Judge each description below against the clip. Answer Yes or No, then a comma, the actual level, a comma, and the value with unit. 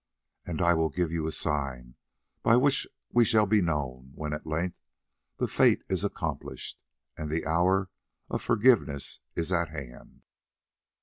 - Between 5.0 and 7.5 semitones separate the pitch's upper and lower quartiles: No, average, 4.2 semitones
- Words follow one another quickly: No, average, 150 wpm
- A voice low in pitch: Yes, very low, 80 Hz